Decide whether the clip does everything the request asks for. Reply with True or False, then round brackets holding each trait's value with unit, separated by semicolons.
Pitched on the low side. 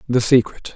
True (120 Hz)